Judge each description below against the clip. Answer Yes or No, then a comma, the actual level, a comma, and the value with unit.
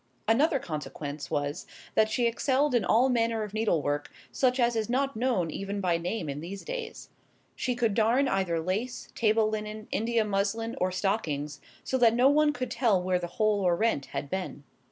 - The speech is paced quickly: No, average, 185 wpm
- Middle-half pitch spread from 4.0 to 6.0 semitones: Yes, average, 4.9 semitones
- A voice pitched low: No, high, 215 Hz